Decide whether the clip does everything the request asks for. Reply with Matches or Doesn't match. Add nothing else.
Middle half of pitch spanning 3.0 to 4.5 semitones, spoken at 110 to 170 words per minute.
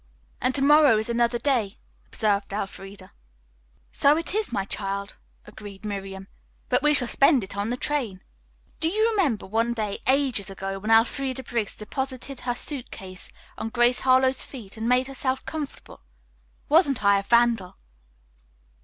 Doesn't match